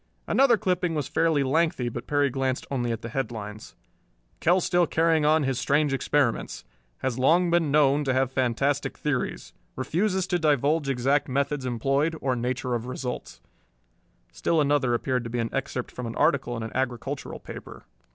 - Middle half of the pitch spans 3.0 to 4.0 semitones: Yes, average, 3.6 semitones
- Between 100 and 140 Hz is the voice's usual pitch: Yes, low, 135 Hz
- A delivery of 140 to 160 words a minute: No, average, 170 wpm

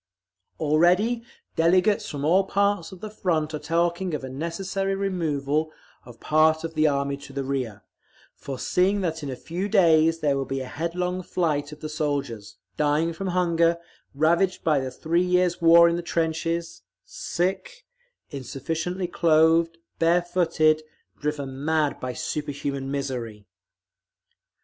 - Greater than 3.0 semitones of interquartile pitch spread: Yes, average, 3.6 semitones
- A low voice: No, medium, 160 Hz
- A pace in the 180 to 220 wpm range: No, average, 140 wpm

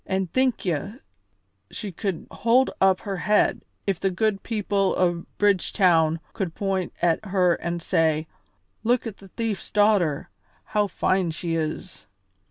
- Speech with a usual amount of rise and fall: Yes, average, 3.2 semitones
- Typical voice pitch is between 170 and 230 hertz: Yes, high, 190 Hz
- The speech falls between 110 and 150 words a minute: Yes, average, 145 wpm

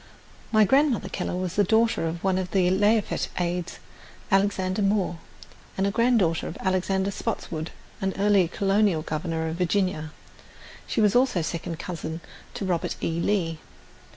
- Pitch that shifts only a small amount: No, average, 3.3 semitones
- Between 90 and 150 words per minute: Yes, average, 140 wpm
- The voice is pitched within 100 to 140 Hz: No, medium, 185 Hz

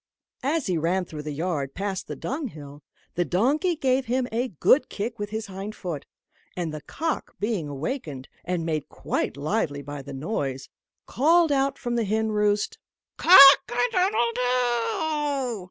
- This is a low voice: No, high, 215 Hz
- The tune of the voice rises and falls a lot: Yes, wide, 8.3 semitones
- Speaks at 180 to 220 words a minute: No, average, 160 wpm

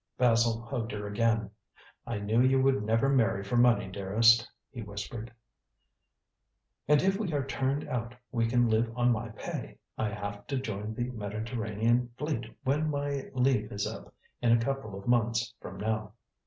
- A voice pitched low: Yes, low, 115 Hz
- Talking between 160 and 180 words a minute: Yes, average, 170 wpm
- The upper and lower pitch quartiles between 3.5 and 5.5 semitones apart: No, average, 2.9 semitones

